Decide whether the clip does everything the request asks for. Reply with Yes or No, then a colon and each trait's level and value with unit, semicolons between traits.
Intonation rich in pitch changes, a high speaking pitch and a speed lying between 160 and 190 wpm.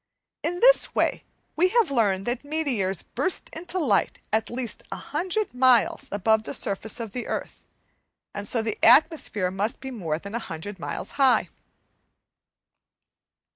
No: wide, 6.5 semitones; high, 235 Hz; average, 140 wpm